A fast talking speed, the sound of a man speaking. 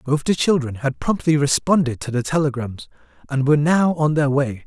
No: average, 195 wpm; male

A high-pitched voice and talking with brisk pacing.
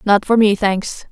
Yes: high, 205 Hz; fast, 215 wpm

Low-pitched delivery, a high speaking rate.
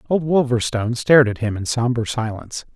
No: low, 120 Hz; average, 175 wpm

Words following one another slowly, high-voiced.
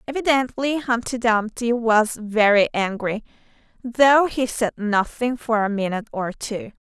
Yes: slow, 130 wpm; high, 230 Hz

